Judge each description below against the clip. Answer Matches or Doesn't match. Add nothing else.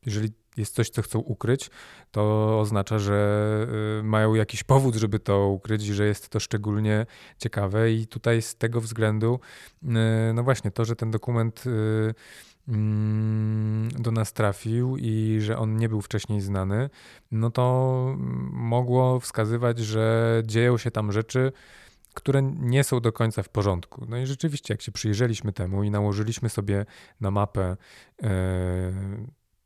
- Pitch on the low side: Matches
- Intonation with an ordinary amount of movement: Doesn't match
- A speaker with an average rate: Matches